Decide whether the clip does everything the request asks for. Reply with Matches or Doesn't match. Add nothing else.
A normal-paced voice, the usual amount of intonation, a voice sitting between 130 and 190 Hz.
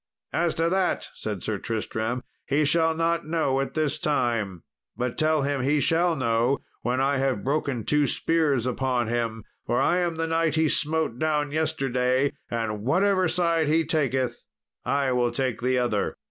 Matches